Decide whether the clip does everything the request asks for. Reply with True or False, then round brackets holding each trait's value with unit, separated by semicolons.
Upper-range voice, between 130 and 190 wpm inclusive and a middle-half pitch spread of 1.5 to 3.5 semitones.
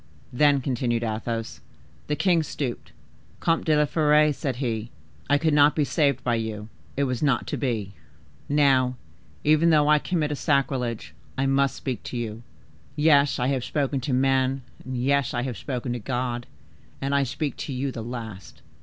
False (135 Hz; 170 wpm; 3.2 semitones)